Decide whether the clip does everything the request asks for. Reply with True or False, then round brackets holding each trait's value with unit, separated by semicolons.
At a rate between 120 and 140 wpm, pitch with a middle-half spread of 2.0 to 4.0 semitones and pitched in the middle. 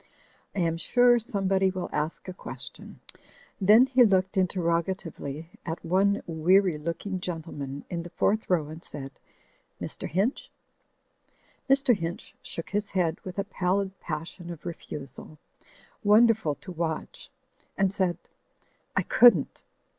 True (135 wpm; 3.4 semitones; 180 Hz)